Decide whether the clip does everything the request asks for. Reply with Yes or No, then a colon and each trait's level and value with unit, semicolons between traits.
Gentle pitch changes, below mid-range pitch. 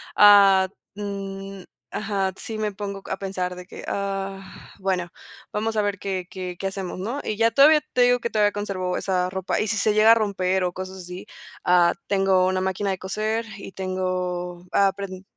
No: narrow, 1.9 semitones; high, 195 Hz